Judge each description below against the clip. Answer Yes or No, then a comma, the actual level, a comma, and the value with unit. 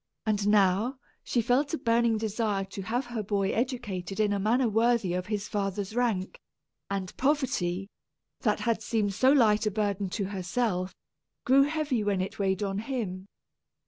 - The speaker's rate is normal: Yes, average, 165 wpm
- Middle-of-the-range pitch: No, high, 210 Hz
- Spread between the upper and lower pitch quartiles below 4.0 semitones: Yes, average, 3.5 semitones